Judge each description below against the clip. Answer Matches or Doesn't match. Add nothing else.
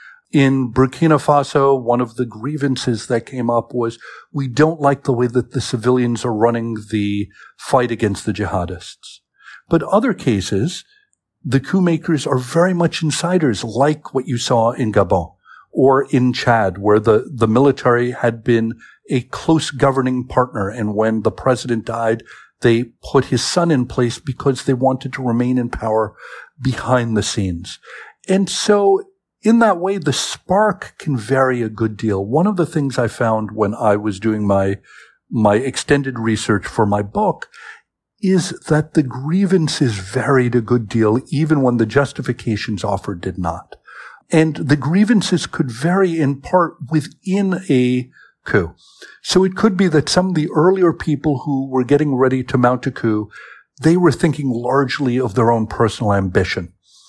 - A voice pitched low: Matches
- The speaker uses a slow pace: Doesn't match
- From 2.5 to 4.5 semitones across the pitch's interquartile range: Doesn't match